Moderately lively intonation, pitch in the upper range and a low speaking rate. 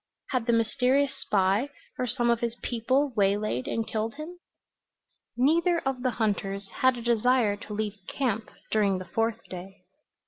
No: average, 3.7 semitones; high, 230 Hz; average, 160 wpm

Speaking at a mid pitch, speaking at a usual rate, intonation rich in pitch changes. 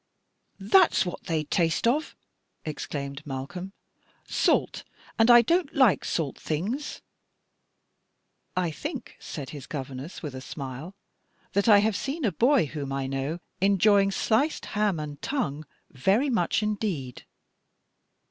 No: medium, 180 Hz; slow, 130 wpm; wide, 7.5 semitones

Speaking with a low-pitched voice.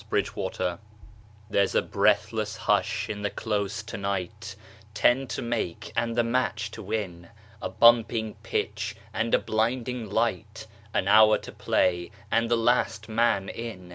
Yes: low, 110 Hz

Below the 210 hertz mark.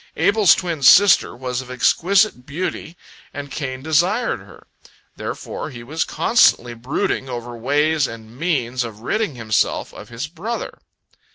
Yes: medium, 140 Hz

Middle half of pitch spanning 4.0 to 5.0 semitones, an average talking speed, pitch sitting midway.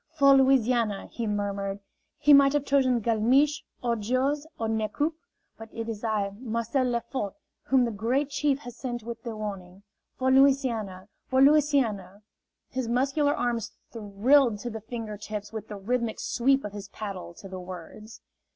No: average, 4.3 semitones; average, 165 wpm; high, 235 Hz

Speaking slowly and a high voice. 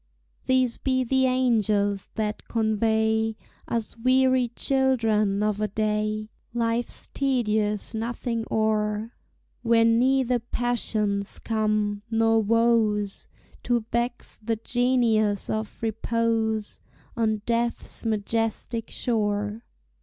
Yes: slow, 95 wpm; high, 225 Hz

